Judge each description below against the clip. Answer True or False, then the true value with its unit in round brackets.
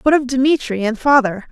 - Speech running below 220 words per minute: True (200 wpm)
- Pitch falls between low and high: False (250 Hz)